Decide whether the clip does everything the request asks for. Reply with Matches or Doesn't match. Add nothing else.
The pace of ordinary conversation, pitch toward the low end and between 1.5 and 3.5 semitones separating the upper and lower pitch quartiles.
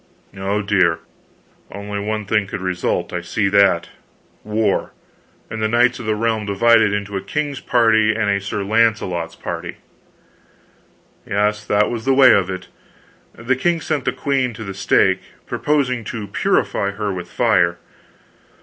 Matches